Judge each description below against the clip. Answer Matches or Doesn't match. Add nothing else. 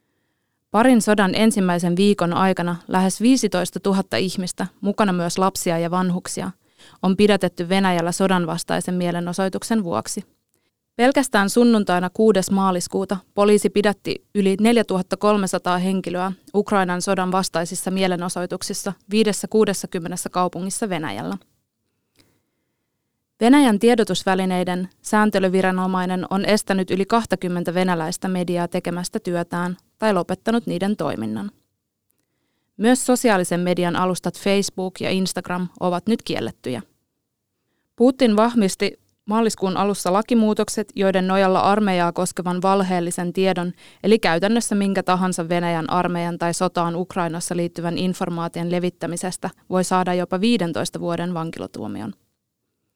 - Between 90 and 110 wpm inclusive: Matches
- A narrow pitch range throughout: Matches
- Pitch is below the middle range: Doesn't match